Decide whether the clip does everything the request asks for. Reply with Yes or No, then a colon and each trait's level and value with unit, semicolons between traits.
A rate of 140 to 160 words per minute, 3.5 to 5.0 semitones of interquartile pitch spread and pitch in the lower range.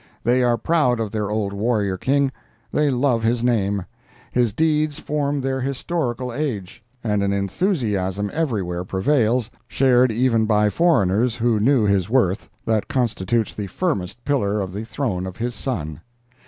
Yes: average, 155 wpm; average, 4.7 semitones; low, 115 Hz